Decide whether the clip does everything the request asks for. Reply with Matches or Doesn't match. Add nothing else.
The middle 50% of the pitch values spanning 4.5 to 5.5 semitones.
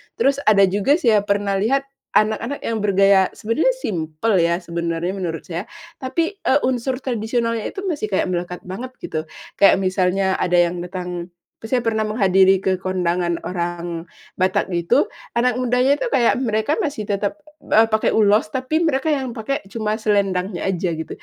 Matches